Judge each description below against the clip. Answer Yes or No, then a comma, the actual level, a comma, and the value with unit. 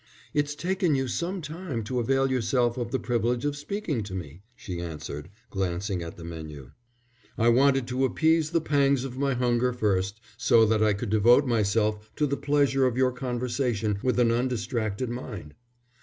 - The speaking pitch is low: Yes, low, 120 Hz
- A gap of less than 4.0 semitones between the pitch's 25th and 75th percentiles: No, average, 4.4 semitones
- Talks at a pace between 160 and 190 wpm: Yes, average, 175 wpm